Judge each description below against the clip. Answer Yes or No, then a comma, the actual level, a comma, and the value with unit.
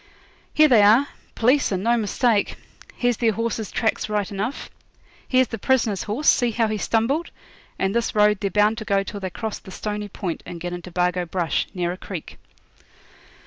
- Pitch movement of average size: Yes, average, 3.4 semitones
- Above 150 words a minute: Yes, average, 185 wpm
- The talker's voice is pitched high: Yes, high, 210 Hz